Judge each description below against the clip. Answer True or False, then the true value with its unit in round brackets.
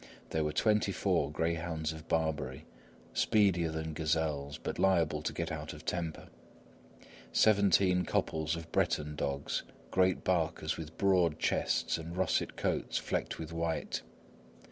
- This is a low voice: True (80 Hz)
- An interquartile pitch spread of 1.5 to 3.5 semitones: True (2.7 semitones)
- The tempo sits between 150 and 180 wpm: False (135 wpm)